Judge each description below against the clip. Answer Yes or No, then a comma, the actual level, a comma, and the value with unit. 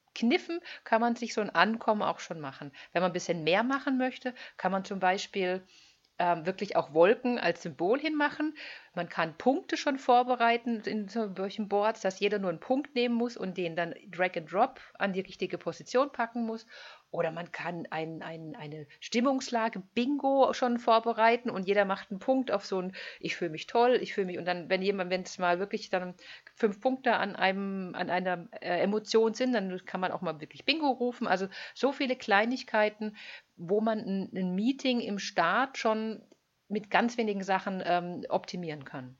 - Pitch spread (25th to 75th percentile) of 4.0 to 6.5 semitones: Yes, average, 4.9 semitones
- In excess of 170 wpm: Yes, fast, 190 wpm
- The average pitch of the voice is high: Yes, high, 205 Hz